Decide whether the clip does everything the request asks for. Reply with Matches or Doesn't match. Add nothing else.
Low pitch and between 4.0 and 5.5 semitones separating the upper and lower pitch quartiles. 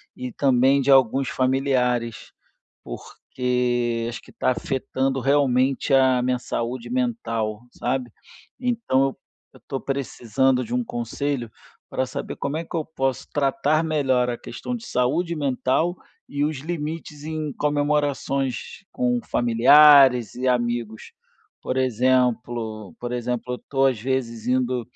Doesn't match